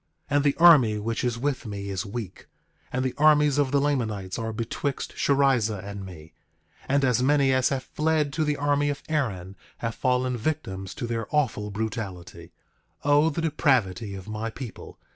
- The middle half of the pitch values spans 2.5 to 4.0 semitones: No, wide, 5.5 semitones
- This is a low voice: Yes, low, 125 Hz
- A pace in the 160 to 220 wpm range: Yes, average, 180 wpm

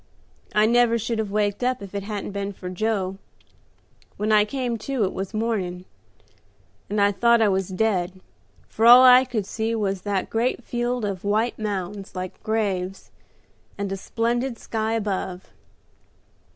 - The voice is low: No, high, 210 Hz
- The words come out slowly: No, average, 160 wpm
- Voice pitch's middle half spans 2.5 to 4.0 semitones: Yes, average, 2.8 semitones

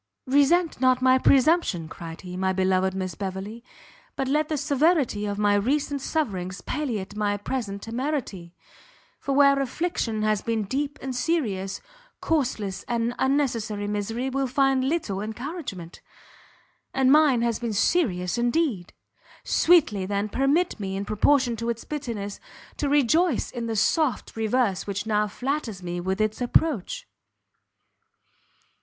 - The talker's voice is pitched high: Yes, high, 235 Hz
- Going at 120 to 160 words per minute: Yes, slow, 135 wpm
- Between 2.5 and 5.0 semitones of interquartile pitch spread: No, wide, 5.6 semitones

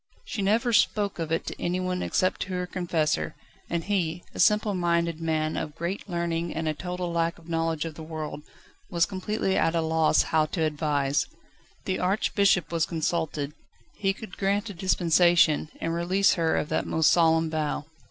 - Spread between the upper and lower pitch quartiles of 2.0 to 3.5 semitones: Yes, narrow, 2.5 semitones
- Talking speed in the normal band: Yes, average, 180 wpm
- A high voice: No, medium, 170 Hz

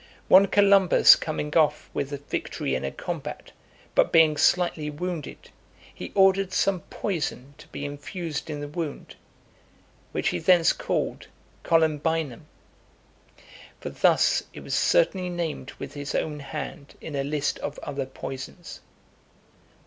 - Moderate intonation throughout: Yes, average, 3.7 semitones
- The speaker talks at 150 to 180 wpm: No, slow, 135 wpm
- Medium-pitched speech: Yes, medium, 155 Hz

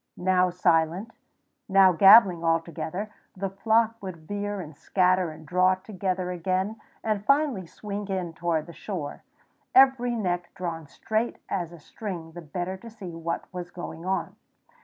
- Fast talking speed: No, average, 155 wpm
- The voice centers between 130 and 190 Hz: Yes, medium, 185 Hz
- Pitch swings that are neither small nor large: Yes, average, 3.1 semitones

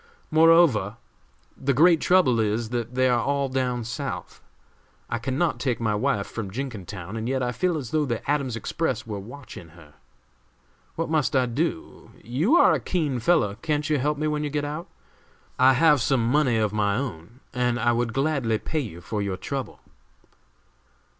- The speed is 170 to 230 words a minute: Yes, average, 180 wpm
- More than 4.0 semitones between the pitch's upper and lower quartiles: Yes, average, 4.7 semitones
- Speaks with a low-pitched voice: Yes, low, 130 Hz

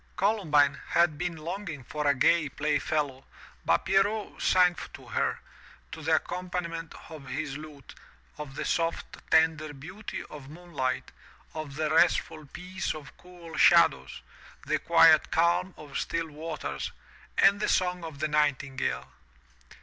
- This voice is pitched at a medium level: Yes, medium, 160 Hz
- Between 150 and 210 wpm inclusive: No, average, 140 wpm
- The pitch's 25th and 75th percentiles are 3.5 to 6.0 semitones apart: No, average, 3.1 semitones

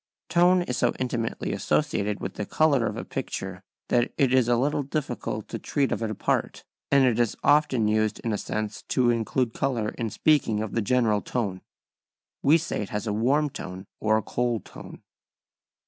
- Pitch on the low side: Yes, low, 120 Hz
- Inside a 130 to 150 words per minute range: No, average, 190 wpm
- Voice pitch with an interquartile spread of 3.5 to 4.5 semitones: Yes, average, 3.9 semitones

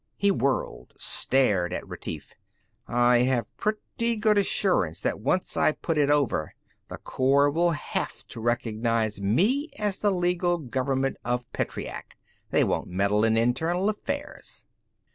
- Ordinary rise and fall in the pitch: No, wide, 7.8 semitones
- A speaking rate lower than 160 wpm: Yes, average, 140 wpm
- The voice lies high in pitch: No, low, 135 Hz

